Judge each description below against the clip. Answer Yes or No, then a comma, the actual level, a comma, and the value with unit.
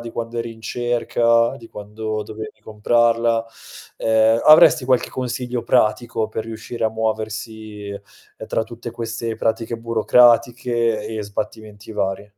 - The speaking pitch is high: No, low, 115 Hz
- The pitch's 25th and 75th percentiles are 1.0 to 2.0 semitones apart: Yes, narrow, 1.4 semitones